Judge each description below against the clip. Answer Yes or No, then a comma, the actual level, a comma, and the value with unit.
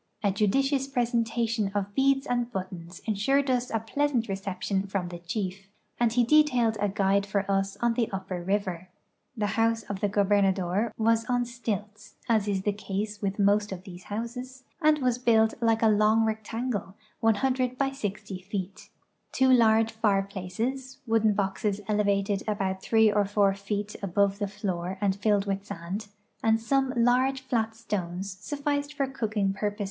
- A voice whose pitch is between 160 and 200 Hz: No, high, 210 Hz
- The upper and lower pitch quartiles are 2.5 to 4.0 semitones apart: Yes, average, 3.2 semitones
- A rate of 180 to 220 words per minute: No, average, 165 wpm